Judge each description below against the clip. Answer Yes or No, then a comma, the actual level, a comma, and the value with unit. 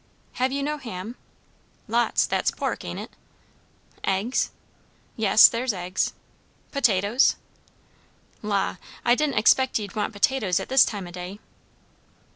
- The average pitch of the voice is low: No, high, 220 Hz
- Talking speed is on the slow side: Yes, slow, 125 wpm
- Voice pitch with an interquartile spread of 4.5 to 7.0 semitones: Yes, average, 4.9 semitones